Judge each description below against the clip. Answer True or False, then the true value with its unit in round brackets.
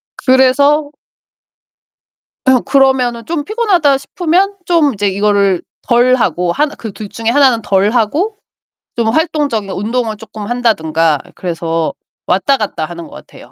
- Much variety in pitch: True (6.0 semitones)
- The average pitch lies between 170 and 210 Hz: False (240 Hz)